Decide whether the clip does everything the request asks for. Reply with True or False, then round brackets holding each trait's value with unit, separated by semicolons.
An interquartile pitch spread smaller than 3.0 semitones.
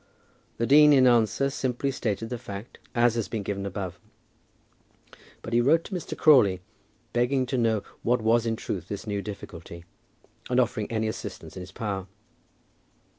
False (3.7 semitones)